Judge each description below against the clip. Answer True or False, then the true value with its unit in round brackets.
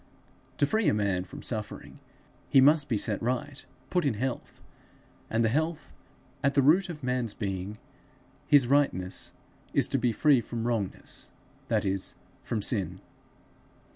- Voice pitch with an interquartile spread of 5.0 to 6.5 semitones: True (5.4 semitones)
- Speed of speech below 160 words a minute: True (150 wpm)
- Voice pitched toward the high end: False (120 Hz)